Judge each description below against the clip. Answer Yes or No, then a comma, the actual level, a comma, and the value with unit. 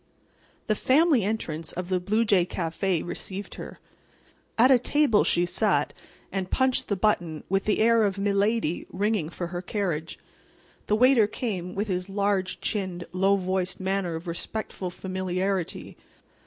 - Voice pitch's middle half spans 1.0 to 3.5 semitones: Yes, average, 3.0 semitones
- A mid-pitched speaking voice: No, high, 195 Hz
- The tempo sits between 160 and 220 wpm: No, average, 150 wpm